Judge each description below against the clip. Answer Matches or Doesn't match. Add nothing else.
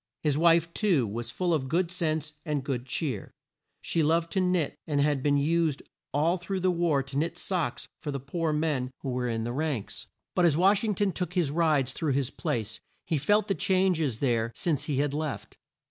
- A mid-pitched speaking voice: Matches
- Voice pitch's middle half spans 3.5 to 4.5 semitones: Matches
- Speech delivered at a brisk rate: Matches